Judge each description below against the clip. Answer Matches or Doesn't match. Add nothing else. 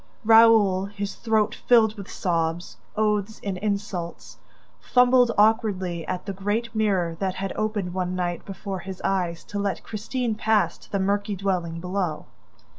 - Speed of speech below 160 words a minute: Matches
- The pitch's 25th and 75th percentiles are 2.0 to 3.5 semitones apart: Matches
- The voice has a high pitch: Matches